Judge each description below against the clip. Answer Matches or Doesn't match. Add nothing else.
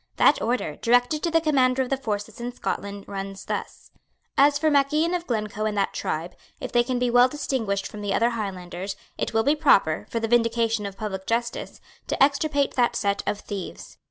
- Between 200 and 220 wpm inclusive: Matches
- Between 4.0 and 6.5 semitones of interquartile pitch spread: Matches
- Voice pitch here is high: Matches